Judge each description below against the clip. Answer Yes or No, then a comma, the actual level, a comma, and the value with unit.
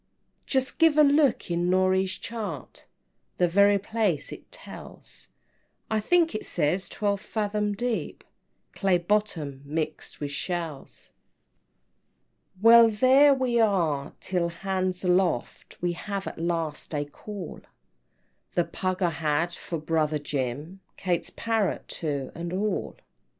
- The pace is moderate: No, slow, 130 wpm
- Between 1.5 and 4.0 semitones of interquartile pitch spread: No, average, 4.4 semitones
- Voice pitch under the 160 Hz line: No, medium, 185 Hz